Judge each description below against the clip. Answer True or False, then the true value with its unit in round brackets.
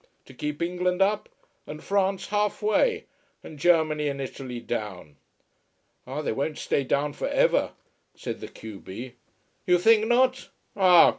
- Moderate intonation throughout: False (6.6 semitones)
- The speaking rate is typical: True (150 wpm)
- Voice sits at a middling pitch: True (160 Hz)